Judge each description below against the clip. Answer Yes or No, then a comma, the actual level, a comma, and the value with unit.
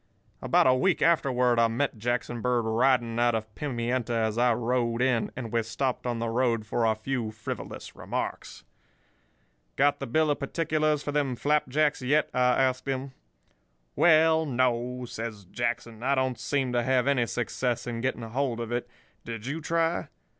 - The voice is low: Yes, low, 125 Hz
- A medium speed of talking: Yes, average, 170 wpm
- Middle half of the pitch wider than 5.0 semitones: No, average, 2.9 semitones